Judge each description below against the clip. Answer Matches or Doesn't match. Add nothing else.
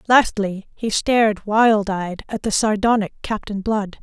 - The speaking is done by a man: Doesn't match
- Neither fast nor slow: Matches